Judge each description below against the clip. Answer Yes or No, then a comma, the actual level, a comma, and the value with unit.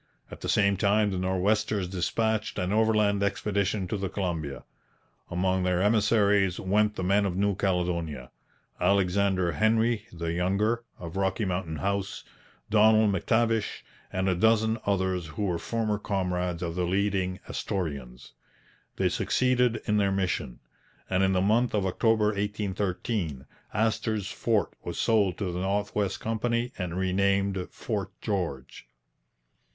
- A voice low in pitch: Yes, low, 100 Hz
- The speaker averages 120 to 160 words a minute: Yes, average, 140 wpm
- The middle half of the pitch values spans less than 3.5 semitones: Yes, average, 2.7 semitones